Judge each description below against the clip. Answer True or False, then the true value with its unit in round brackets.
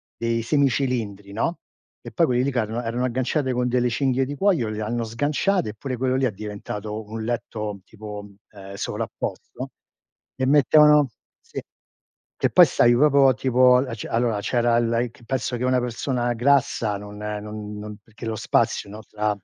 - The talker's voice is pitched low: True (120 Hz)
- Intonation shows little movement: False (3.4 semitones)